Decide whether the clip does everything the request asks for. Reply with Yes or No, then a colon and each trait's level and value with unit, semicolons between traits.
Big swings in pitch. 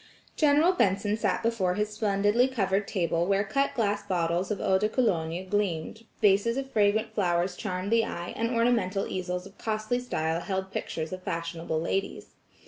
No: average, 3.8 semitones